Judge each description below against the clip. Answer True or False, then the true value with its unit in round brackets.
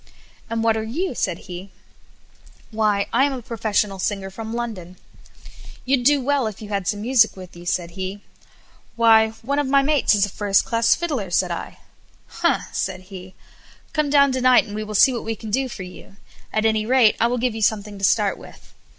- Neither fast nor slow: False (210 wpm)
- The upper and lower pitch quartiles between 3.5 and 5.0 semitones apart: True (4.0 semitones)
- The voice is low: False (220 Hz)